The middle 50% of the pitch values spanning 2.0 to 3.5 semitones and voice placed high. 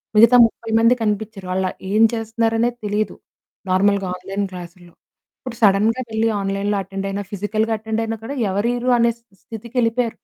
Yes: narrow, 2.5 semitones; high, 215 Hz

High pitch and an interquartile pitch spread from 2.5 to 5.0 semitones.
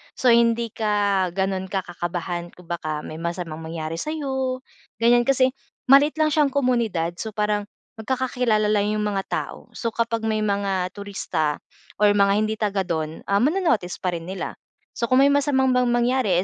No: high, 210 Hz; wide, 5.4 semitones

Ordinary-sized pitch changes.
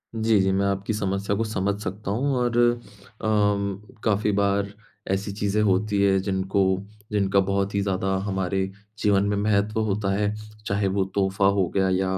No: narrow, 1.3 semitones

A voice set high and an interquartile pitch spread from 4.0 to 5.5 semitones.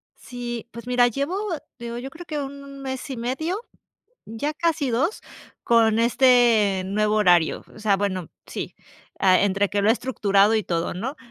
Yes: high, 235 Hz; average, 4.8 semitones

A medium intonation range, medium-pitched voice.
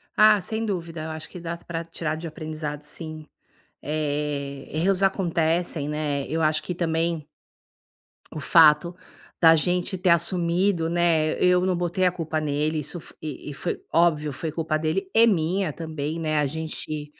No: narrow, 2.1 semitones; medium, 160 Hz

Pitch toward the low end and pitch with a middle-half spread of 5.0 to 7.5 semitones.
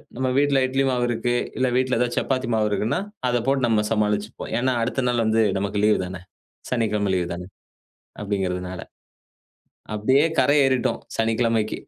No: low, 115 Hz; average, 3.6 semitones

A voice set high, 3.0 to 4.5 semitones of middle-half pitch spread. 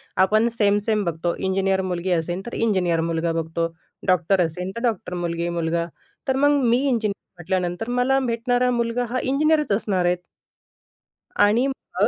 No: high, 195 Hz; average, 5.2 semitones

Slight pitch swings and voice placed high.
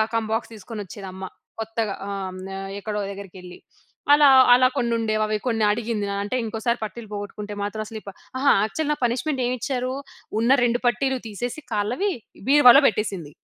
No: average, 3.0 semitones; high, 220 Hz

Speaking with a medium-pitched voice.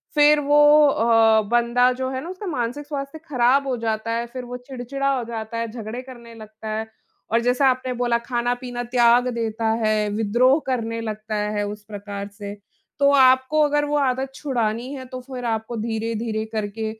No: high, 240 Hz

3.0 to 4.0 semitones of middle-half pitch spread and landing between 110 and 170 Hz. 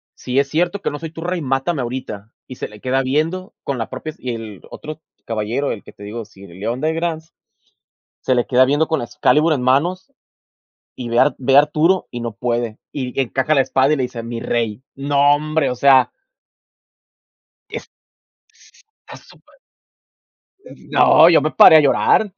No: average, 4.4 semitones; low, 135 Hz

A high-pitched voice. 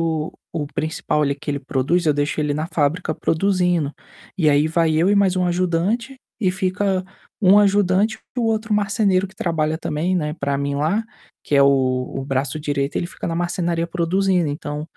No: medium, 165 Hz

